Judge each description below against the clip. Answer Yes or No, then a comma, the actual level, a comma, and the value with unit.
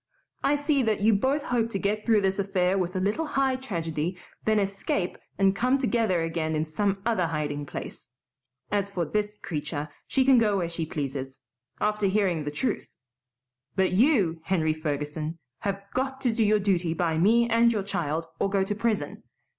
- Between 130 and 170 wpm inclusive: No, average, 185 wpm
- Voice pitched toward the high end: Yes, high, 195 Hz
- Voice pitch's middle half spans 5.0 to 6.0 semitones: Yes, average, 5.3 semitones